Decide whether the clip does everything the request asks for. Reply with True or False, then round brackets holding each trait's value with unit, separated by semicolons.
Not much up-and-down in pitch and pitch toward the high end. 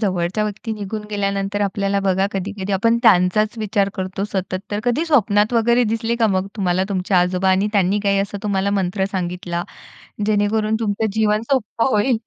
True (2.2 semitones; 200 Hz)